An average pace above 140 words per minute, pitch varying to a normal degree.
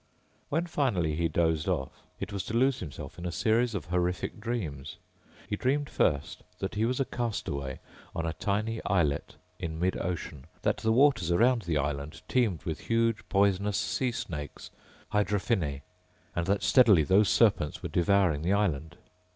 No: average, 165 wpm; wide, 5.9 semitones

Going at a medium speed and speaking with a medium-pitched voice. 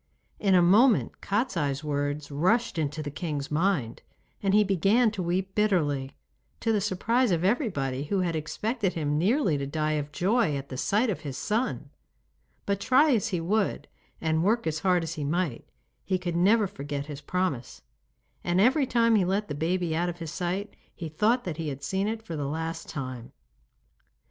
Yes: average, 190 wpm; medium, 175 Hz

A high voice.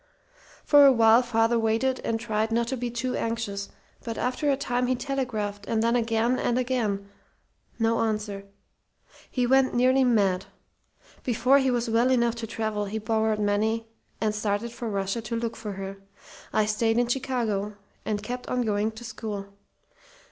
Yes: high, 225 Hz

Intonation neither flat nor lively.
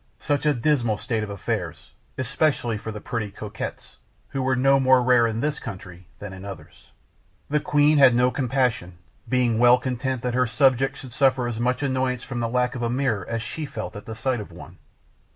Yes: average, 3.0 semitones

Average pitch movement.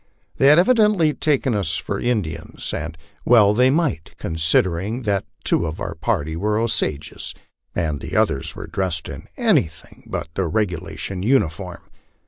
No: wide, 7.2 semitones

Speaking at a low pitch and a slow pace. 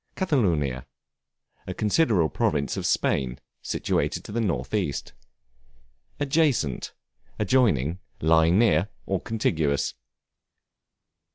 Yes: very low, 90 Hz; slow, 90 wpm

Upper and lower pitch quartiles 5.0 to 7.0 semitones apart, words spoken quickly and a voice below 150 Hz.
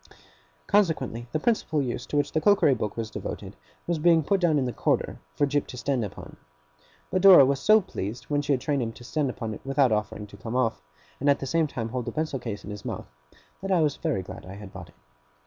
Yes: wide, 5.5 semitones; fast, 250 wpm; low, 135 Hz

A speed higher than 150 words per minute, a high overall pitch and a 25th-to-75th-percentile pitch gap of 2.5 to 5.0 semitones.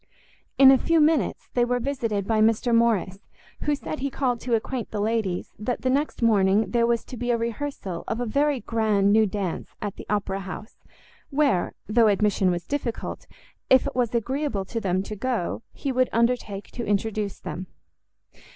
Yes: average, 185 wpm; high, 230 Hz; average, 3.8 semitones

